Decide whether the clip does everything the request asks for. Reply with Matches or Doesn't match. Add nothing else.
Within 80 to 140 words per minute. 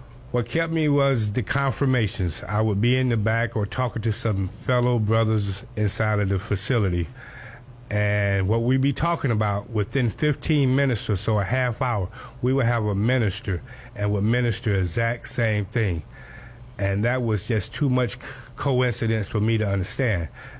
Doesn't match